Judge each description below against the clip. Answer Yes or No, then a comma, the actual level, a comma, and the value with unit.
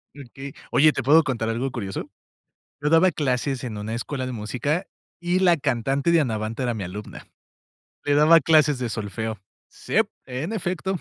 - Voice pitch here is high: No, low, 135 Hz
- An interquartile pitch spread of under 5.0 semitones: No, wide, 5.4 semitones